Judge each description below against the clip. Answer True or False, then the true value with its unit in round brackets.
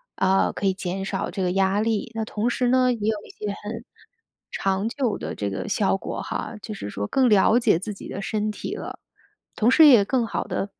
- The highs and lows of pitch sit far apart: False (3.0 semitones)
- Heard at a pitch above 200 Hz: True (210 Hz)